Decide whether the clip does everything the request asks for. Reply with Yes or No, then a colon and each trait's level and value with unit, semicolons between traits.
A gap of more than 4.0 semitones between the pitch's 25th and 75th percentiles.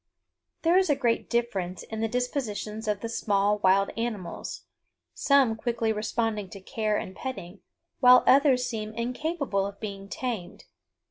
No: average, 3.6 semitones